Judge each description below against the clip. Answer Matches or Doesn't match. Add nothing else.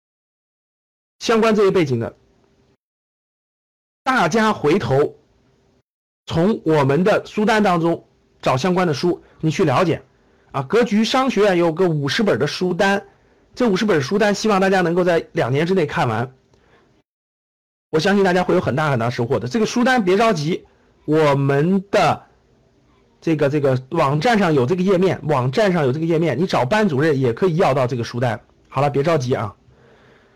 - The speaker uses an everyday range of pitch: Doesn't match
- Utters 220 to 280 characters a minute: Matches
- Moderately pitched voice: Matches